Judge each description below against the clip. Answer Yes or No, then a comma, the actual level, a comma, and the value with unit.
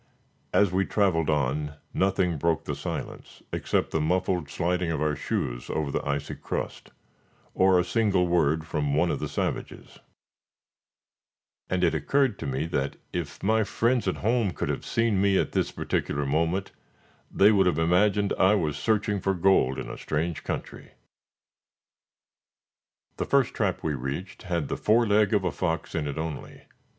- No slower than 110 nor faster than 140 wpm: No, average, 165 wpm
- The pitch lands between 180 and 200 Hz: No, very low, 85 Hz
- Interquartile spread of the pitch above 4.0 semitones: Yes, average, 4.5 semitones